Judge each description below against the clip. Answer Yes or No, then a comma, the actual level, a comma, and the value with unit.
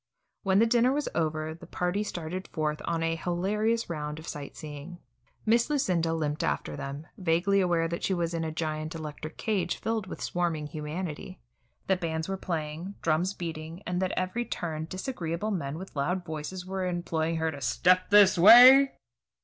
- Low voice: No, medium, 170 Hz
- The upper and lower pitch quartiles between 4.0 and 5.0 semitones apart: No, average, 3.3 semitones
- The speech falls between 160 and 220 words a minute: Yes, average, 180 wpm